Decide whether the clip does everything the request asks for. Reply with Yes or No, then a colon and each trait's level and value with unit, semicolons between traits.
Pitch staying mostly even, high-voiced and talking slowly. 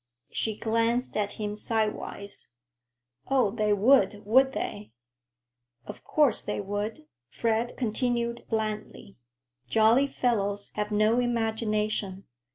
Yes: narrow, 2.2 semitones; high, 220 Hz; slow, 105 wpm